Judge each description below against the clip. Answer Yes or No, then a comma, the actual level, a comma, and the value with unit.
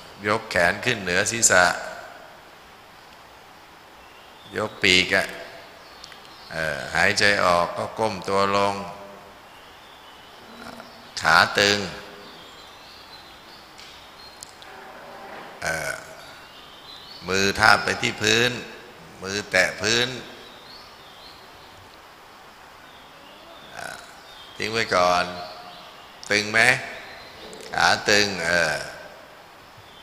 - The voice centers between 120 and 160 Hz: No, low, 100 Hz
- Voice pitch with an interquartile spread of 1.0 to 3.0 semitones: Yes, average, 2.7 semitones